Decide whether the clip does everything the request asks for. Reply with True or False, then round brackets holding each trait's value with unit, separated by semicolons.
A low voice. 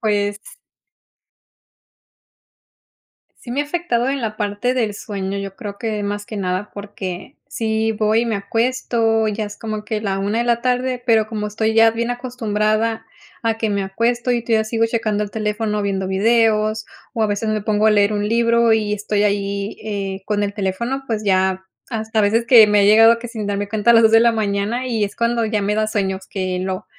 False (215 Hz)